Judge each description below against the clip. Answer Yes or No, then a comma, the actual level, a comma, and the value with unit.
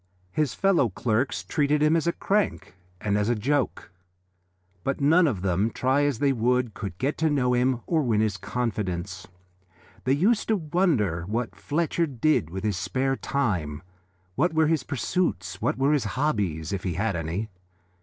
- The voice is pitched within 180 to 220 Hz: No, low, 125 Hz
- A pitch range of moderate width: No, wide, 6.9 semitones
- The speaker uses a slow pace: No, average, 175 wpm